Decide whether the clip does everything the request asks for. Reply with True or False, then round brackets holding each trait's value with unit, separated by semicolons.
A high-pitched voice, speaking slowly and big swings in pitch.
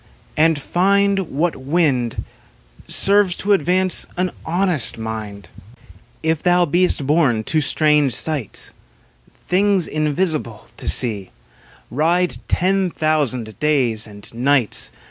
False (155 Hz; 105 wpm; 6.3 semitones)